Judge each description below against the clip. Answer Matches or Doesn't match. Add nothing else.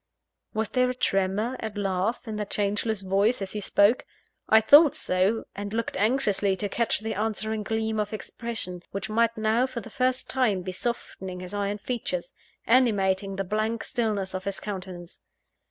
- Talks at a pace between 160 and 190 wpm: Matches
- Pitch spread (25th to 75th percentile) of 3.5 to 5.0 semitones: Doesn't match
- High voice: Matches